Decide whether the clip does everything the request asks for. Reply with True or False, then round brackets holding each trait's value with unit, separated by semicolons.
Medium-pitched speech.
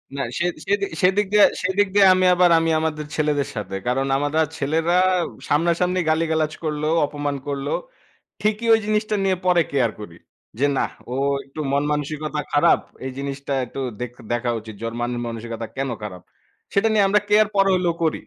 True (155 Hz)